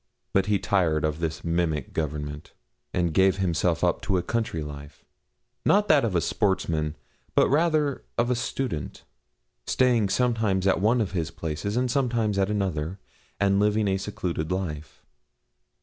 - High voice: No, very low, 95 Hz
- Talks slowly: No, average, 155 wpm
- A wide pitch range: Yes, wide, 5.7 semitones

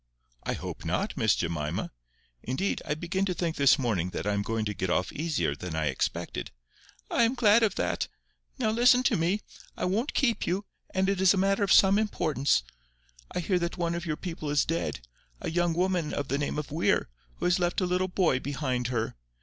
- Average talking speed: No, fast, 215 wpm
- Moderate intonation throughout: No, wide, 6.8 semitones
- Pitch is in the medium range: Yes, medium, 170 Hz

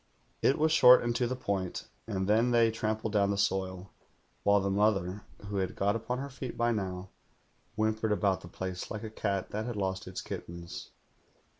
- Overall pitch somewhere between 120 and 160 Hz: No, low, 105 Hz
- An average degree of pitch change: Yes, average, 3.1 semitones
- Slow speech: No, average, 190 wpm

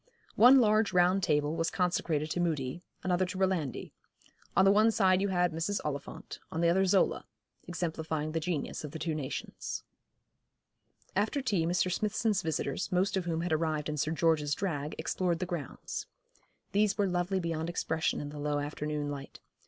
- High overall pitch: No, medium, 170 Hz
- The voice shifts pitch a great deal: No, average, 3.7 semitones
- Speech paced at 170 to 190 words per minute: Yes, average, 175 wpm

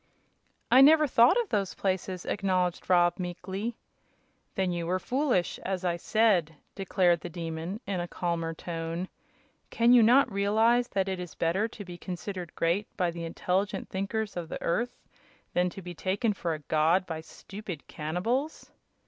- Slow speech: No, average, 165 wpm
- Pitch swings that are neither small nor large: Yes, average, 3.6 semitones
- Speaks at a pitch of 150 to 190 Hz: Yes, medium, 185 Hz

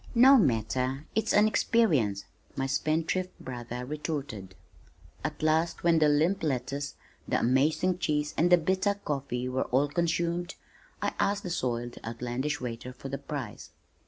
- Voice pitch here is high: No, medium, 145 Hz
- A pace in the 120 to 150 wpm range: Yes, average, 140 wpm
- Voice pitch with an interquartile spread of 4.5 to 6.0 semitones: Yes, average, 5.1 semitones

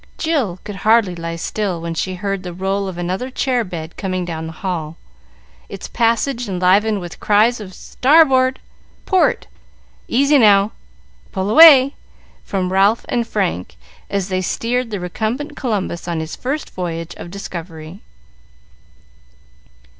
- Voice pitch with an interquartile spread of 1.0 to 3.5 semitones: No, average, 5.1 semitones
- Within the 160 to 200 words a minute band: No, average, 140 wpm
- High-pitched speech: Yes, high, 195 Hz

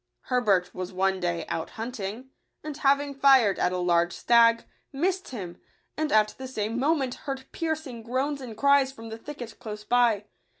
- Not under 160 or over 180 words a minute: Yes, average, 170 wpm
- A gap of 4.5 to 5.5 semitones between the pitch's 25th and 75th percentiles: Yes, average, 4.9 semitones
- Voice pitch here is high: Yes, high, 240 Hz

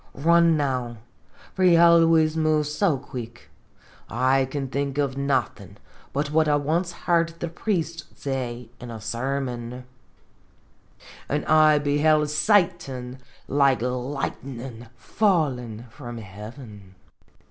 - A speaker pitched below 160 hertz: Yes, medium, 140 Hz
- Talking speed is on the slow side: Yes, slow, 125 wpm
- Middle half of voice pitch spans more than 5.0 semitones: No, average, 4.1 semitones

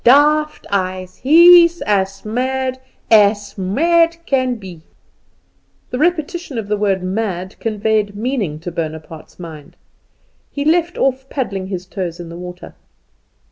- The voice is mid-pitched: No, high, 210 Hz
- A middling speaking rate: No, slow, 130 wpm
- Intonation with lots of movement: Yes, wide, 6.7 semitones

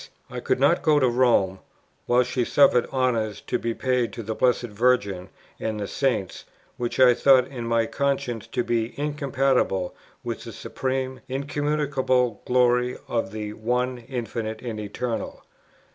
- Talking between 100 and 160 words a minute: Yes, average, 155 wpm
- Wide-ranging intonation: No, narrow, 2.6 semitones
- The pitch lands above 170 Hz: No, low, 125 Hz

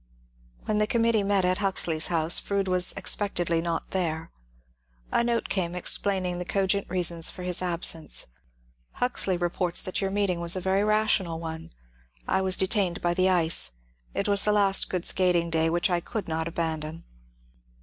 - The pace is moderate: Yes, average, 170 wpm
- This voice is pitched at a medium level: Yes, medium, 180 Hz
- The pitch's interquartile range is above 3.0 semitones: No, average, 2.7 semitones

